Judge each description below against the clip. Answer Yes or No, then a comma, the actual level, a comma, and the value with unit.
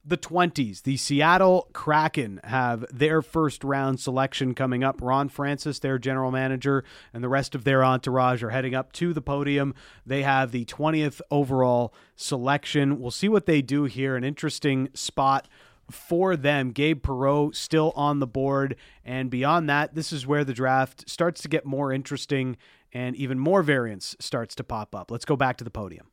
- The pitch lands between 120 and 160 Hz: Yes, low, 135 Hz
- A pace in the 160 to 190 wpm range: Yes, average, 180 wpm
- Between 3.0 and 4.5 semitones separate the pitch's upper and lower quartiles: No, narrow, 2.4 semitones